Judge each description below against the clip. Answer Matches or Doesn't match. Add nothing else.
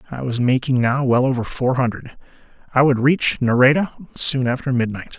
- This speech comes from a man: Matches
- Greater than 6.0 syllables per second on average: Doesn't match